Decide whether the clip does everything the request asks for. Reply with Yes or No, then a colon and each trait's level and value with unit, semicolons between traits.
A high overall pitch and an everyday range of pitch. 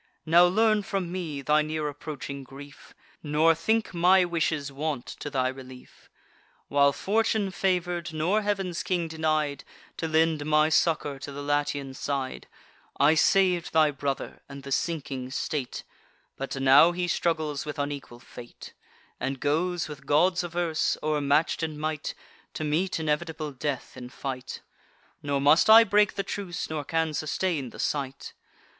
No: medium, 155 Hz; average, 3.6 semitones